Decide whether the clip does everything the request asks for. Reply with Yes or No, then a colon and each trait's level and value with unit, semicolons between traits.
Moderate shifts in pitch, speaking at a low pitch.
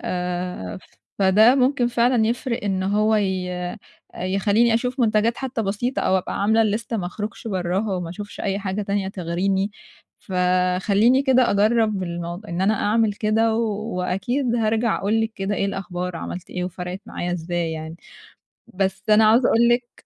No: average, 3.6 semitones; high, 205 Hz